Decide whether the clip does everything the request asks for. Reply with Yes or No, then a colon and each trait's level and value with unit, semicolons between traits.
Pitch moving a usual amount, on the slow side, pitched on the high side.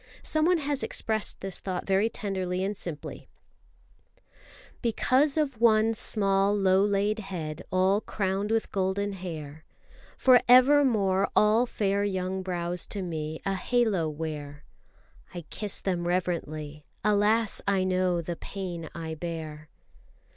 Yes: average, 3.6 semitones; slow, 125 wpm; high, 195 Hz